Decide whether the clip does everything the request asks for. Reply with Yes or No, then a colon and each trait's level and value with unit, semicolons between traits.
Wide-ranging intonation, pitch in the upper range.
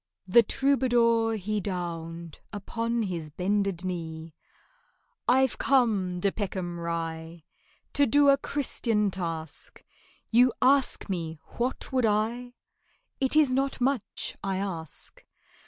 Yes: wide, 6.3 semitones; high, 205 Hz